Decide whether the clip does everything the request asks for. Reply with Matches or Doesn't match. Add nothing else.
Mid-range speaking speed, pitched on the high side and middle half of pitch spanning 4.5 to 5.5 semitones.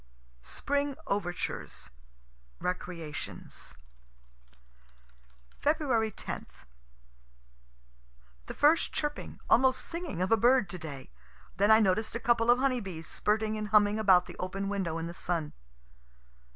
Doesn't match